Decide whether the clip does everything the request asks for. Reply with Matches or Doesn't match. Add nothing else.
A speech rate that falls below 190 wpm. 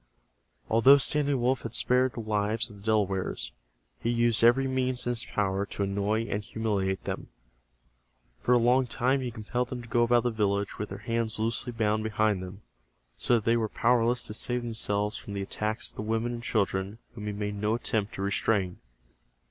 Doesn't match